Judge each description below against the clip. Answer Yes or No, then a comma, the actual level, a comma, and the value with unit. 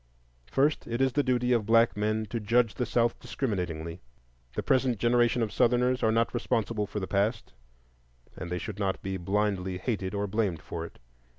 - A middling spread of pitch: Yes, average, 3.6 semitones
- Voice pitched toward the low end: Yes, low, 110 Hz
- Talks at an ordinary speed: Yes, average, 185 wpm